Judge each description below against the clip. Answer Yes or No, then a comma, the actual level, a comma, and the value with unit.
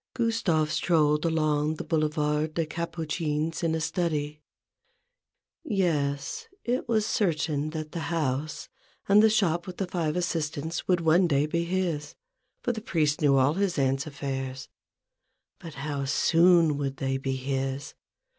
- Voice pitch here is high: No, medium, 155 Hz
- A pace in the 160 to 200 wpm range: No, average, 145 wpm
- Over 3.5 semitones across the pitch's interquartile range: No, average, 2.9 semitones